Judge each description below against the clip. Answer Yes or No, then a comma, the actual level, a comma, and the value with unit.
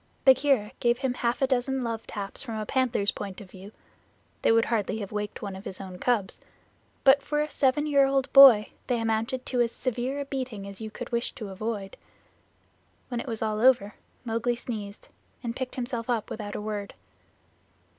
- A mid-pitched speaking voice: No, high, 230 Hz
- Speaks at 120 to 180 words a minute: No, average, 195 wpm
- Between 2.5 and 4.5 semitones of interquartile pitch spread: Yes, average, 3.7 semitones